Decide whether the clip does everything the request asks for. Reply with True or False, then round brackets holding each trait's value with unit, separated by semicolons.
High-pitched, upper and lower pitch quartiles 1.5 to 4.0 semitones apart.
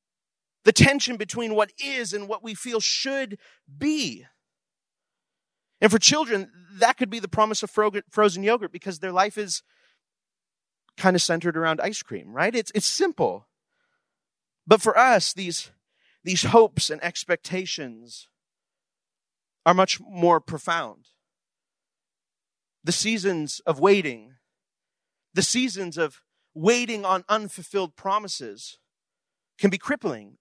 False (200 Hz; 4.4 semitones)